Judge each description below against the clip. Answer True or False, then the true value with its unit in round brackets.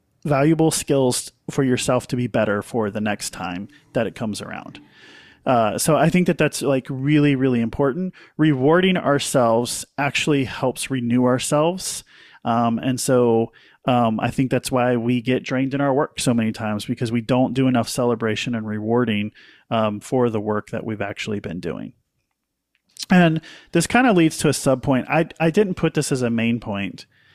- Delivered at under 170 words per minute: False (180 wpm)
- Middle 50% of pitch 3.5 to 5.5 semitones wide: True (4.2 semitones)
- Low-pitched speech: True (130 Hz)